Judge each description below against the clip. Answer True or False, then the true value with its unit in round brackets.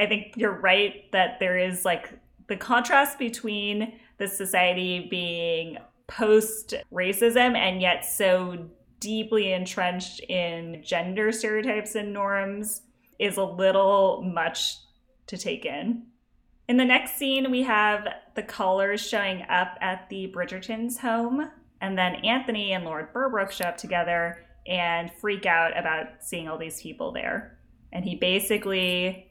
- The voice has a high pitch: True (195 Hz)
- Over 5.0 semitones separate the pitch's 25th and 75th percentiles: False (3.3 semitones)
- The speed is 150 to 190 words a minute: False (140 wpm)